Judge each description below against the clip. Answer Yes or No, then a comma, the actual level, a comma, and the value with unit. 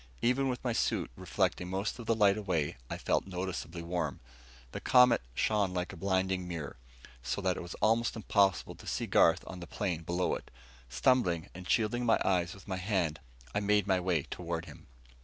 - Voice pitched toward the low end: Yes, very low, 95 Hz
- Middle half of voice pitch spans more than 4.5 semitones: No, average, 3.3 semitones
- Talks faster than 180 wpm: Yes, average, 195 wpm